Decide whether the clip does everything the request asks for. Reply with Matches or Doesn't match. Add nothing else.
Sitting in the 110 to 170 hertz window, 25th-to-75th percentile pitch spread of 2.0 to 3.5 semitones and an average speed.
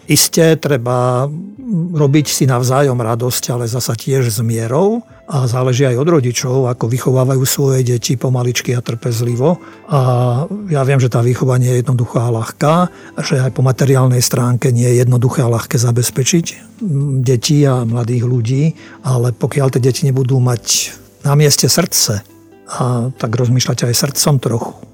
Matches